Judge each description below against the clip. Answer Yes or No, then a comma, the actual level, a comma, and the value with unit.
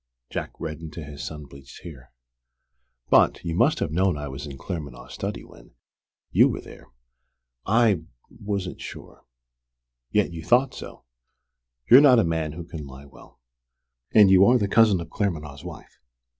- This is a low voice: Yes, very low, 85 Hz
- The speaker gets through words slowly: No, average, 160 wpm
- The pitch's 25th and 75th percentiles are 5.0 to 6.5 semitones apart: Yes, wide, 5.5 semitones